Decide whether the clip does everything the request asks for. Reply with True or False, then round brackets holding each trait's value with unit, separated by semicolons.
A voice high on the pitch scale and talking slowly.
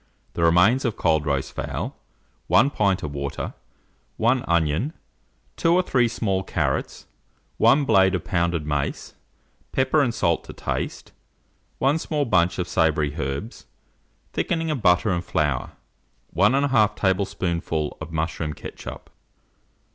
False (95 Hz; 130 wpm)